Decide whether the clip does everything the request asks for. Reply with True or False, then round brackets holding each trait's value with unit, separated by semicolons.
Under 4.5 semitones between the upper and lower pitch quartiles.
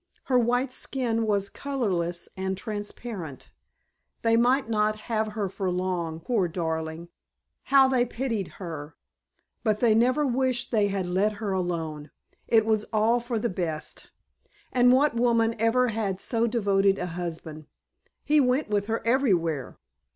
False (4.9 semitones)